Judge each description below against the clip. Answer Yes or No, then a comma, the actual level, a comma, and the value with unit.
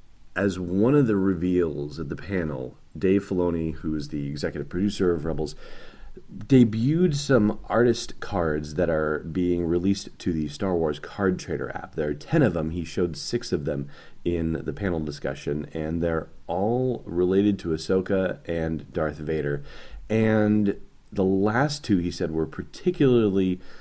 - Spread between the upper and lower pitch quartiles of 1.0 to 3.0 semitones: No, average, 4.5 semitones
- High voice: No, very low, 90 Hz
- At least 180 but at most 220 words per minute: No, average, 160 wpm